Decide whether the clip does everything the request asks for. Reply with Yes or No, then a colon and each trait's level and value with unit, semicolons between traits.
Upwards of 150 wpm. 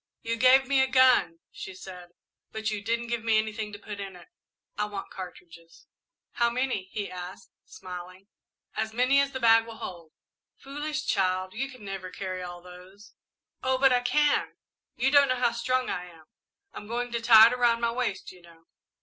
Yes: average, 190 wpm